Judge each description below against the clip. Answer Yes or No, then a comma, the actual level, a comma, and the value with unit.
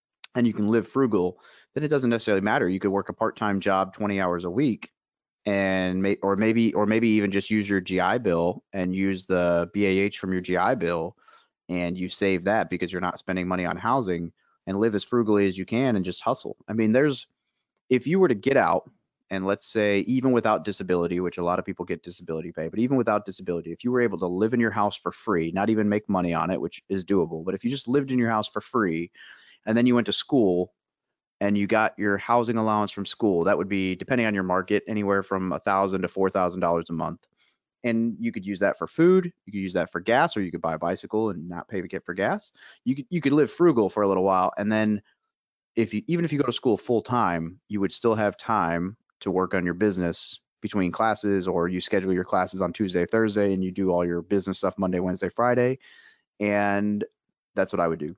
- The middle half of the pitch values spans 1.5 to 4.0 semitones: Yes, average, 3.3 semitones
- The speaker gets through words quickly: Yes, fast, 240 wpm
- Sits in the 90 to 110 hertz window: Yes, low, 100 Hz